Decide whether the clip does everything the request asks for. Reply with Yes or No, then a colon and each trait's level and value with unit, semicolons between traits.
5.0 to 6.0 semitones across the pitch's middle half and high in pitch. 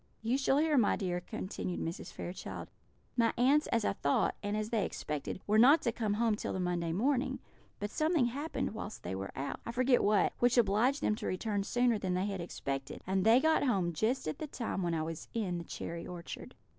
Yes: wide, 5.5 semitones; high, 210 Hz